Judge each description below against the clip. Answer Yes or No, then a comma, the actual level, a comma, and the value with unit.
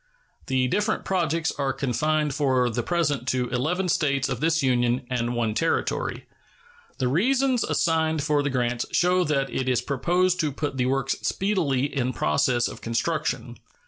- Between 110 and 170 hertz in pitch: Yes, medium, 140 Hz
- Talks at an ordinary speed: Yes, average, 160 wpm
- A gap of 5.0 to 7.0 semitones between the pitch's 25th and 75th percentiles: No, average, 4.5 semitones